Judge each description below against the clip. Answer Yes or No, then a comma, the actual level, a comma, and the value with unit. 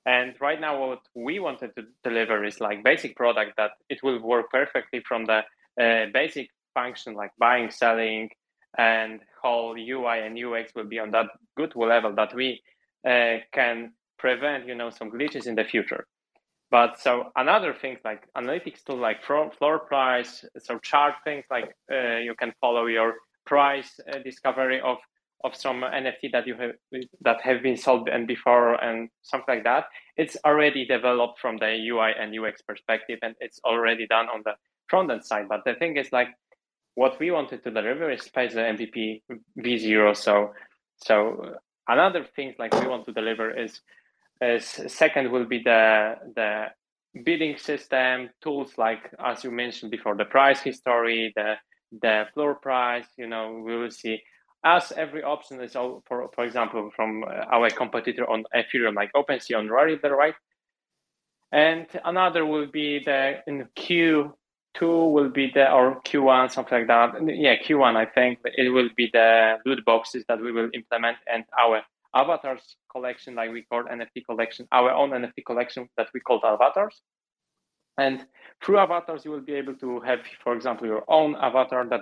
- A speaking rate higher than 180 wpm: No, average, 175 wpm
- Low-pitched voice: Yes, low, 125 Hz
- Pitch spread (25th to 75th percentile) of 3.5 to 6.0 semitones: No, average, 3.0 semitones